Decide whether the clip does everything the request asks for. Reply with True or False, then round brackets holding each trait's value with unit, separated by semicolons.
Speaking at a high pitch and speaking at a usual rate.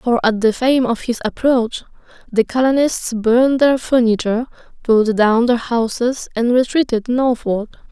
True (240 Hz; 145 wpm)